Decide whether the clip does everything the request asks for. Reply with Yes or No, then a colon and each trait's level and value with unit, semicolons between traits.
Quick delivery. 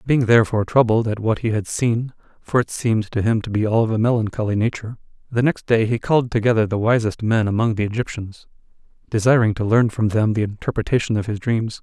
Yes: fast, 215 wpm